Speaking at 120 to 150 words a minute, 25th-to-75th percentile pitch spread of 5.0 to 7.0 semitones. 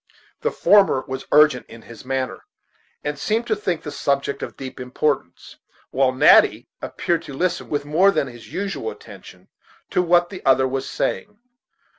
No: average, 165 wpm; wide, 5.4 semitones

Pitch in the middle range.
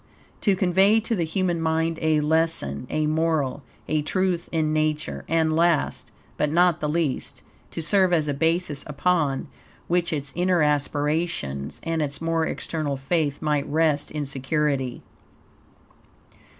Yes: medium, 160 Hz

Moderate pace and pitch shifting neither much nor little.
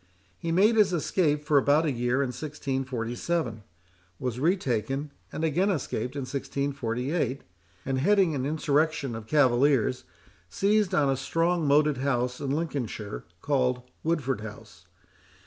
No: slow, 130 wpm; average, 4.0 semitones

